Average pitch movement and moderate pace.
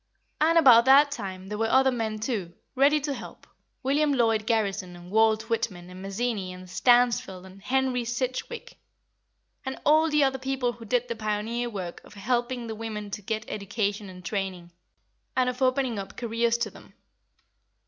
Yes: average, 4.2 semitones; average, 170 wpm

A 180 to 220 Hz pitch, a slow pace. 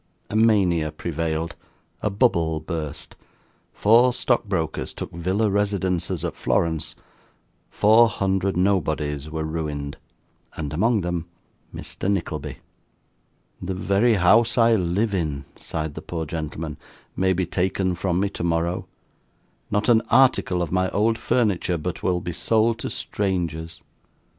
No: very low, 90 Hz; slow, 130 wpm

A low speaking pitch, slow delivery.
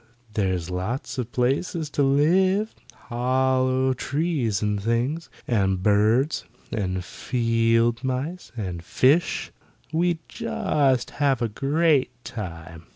Yes: low, 125 Hz; slow, 105 wpm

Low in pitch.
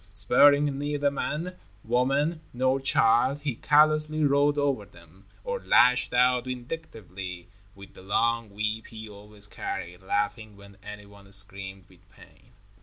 Yes: low, 115 Hz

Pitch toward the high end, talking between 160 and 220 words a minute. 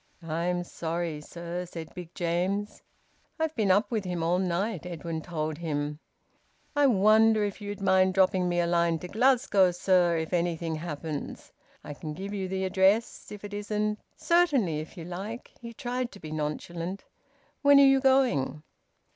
No: medium, 180 Hz; average, 170 wpm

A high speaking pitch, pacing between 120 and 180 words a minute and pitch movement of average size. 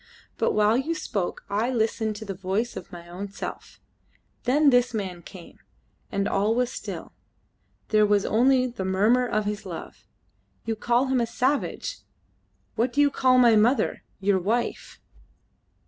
Yes: high, 225 Hz; average, 160 wpm; average, 3.7 semitones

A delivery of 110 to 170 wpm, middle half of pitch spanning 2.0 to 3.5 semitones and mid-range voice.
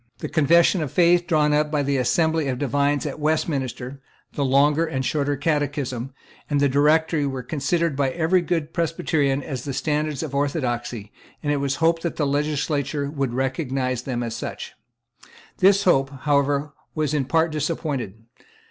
Yes: average, 165 wpm; average, 2.8 semitones; medium, 145 Hz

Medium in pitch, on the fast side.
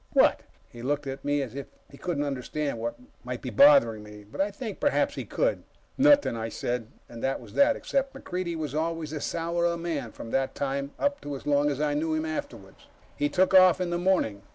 Yes: medium, 150 Hz; fast, 220 wpm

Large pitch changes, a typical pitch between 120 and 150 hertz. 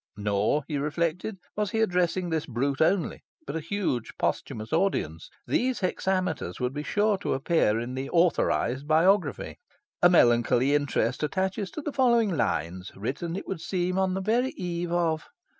No: wide, 6.0 semitones; medium, 170 Hz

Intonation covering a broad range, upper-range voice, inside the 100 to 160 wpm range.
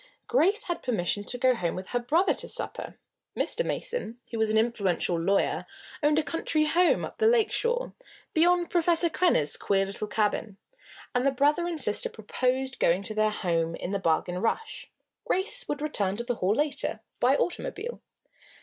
No: wide, 8.8 semitones; very high, 250 Hz; average, 175 wpm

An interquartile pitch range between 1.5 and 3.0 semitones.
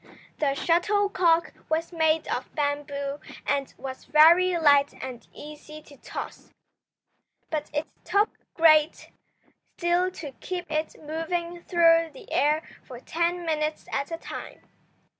Yes: narrow, 2.6 semitones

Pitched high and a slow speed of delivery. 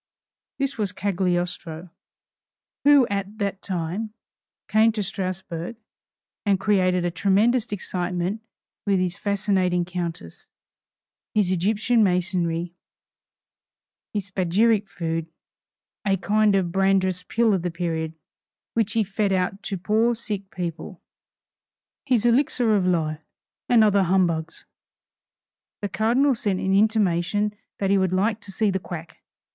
Yes: high, 195 Hz; slow, 125 wpm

